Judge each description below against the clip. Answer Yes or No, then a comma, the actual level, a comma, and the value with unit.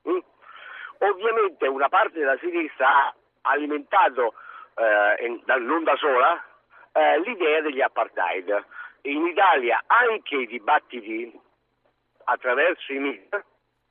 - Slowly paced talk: Yes, slow, 110 wpm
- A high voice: Yes, very high, 335 Hz